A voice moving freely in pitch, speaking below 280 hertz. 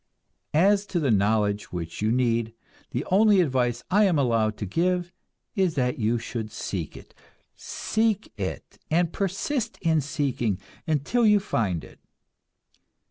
Yes: wide, 9.0 semitones; low, 135 Hz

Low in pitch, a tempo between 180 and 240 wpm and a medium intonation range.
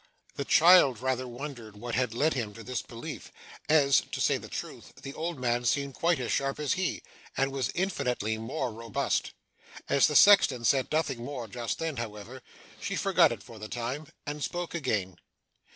Yes: low, 130 Hz; average, 185 wpm; average, 4.0 semitones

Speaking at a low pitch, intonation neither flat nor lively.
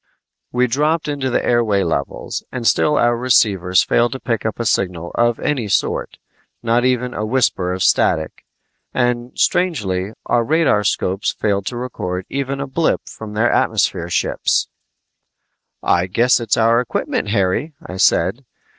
Yes: low, 115 Hz; average, 4.5 semitones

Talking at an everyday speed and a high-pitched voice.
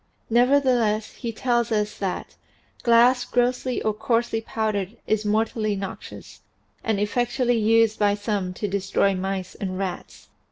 No: slow, 130 wpm; high, 220 Hz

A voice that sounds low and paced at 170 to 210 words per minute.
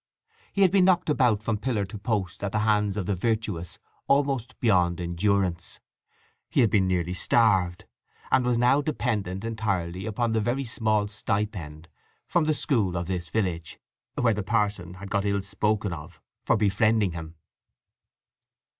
No: low, 105 Hz; average, 160 wpm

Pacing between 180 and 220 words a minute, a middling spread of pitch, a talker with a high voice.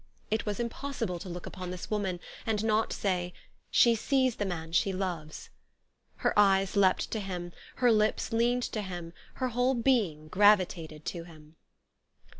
No: average, 165 wpm; average, 4.2 semitones; high, 195 Hz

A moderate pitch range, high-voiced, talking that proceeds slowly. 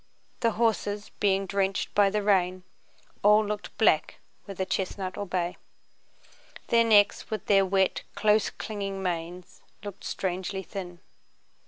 No: narrow, 1.9 semitones; high, 195 Hz; slow, 130 wpm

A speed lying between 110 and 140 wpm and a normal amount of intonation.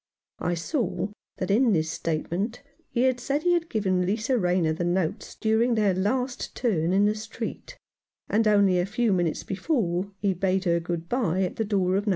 No: average, 190 wpm; average, 4.3 semitones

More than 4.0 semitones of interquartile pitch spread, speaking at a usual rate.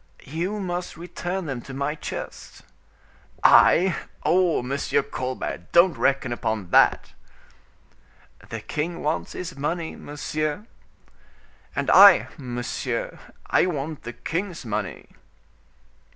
No: average, 5.0 semitones; slow, 110 wpm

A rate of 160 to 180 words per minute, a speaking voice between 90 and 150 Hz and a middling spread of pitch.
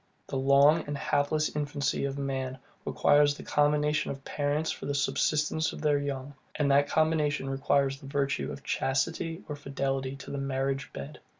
No: average, 170 wpm; medium, 140 Hz; narrow, 1.4 semitones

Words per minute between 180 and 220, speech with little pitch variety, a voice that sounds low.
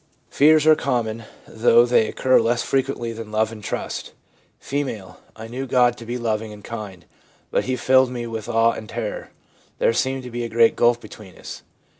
Yes: average, 195 wpm; narrow, 2.1 semitones; low, 115 Hz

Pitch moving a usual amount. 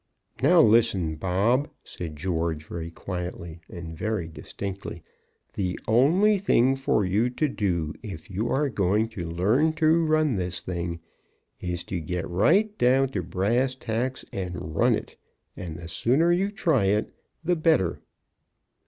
No: wide, 7.4 semitones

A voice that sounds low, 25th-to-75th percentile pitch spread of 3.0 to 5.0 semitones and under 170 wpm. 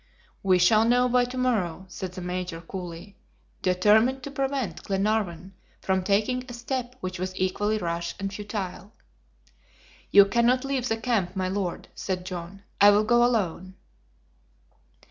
No: high, 200 Hz; average, 4.5 semitones; average, 145 wpm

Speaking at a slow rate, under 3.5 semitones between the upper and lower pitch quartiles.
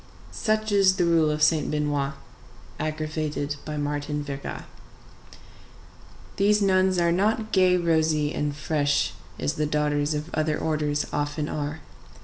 Yes: slow, 130 wpm; average, 2.7 semitones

